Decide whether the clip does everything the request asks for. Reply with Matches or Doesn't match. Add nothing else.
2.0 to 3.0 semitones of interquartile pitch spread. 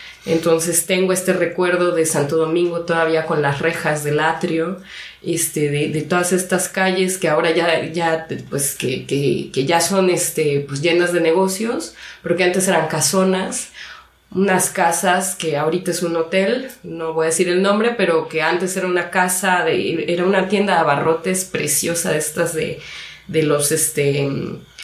Matches